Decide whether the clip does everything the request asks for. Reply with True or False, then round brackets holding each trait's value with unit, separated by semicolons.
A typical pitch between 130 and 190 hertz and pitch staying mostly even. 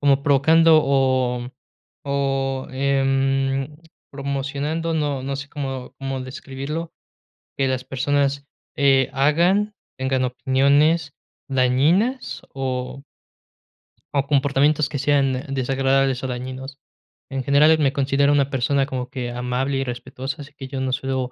True (135 Hz; 1.4 semitones)